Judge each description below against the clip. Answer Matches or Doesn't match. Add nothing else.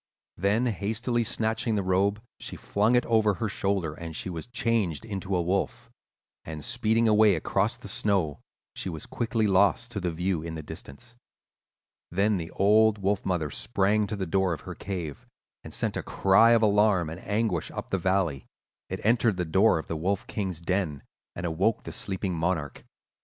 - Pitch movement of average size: Matches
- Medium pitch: Doesn't match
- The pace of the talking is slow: Doesn't match